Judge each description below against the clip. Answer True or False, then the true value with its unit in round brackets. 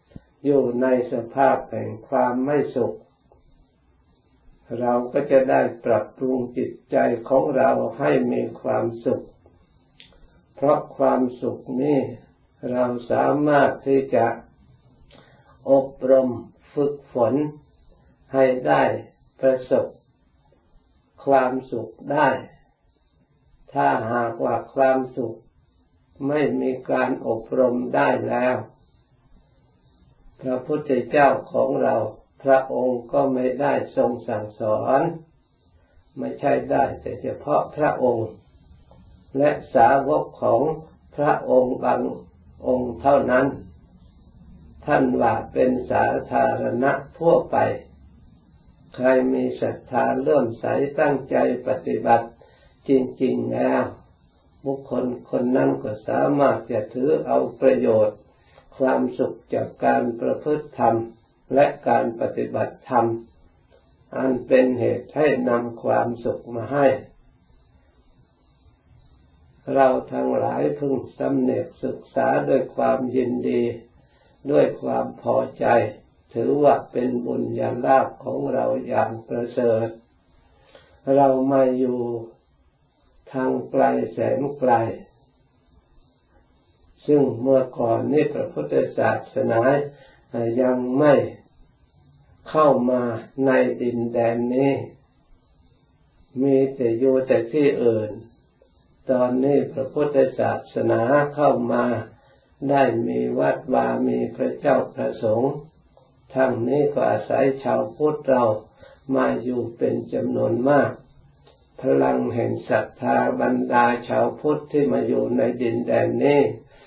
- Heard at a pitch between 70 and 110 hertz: False (125 Hz)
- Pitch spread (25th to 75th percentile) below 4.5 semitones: True (3.8 semitones)